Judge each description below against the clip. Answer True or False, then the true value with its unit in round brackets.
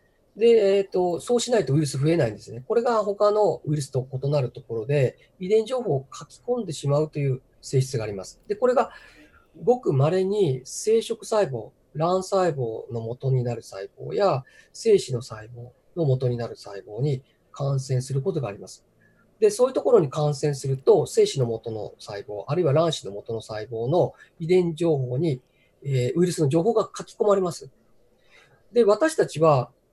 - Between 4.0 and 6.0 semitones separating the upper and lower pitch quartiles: False (7.8 semitones)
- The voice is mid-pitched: True (150 Hz)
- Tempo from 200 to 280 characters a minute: False (345 characters per minute)